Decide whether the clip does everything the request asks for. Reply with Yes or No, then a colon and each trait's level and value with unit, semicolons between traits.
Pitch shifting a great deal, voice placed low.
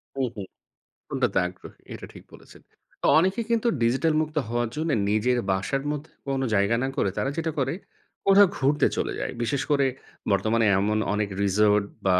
Yes: wide, 6.3 semitones; low, 125 Hz